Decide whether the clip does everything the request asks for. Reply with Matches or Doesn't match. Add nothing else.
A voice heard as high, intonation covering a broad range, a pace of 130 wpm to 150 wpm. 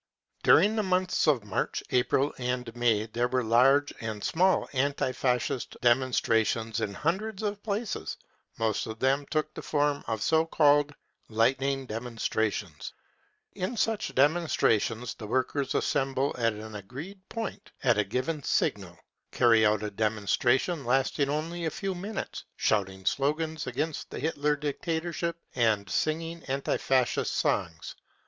Doesn't match